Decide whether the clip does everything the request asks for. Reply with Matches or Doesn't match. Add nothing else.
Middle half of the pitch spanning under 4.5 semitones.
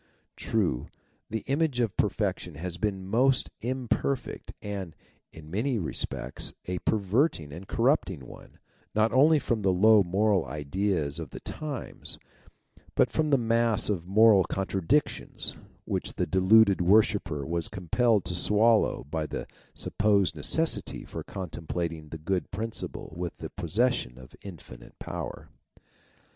Doesn't match